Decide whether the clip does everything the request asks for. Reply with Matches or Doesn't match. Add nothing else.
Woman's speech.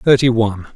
Doesn't match